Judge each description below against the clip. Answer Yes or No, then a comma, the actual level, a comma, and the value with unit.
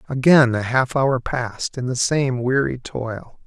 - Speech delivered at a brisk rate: No, average, 175 wpm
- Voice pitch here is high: No, low, 125 Hz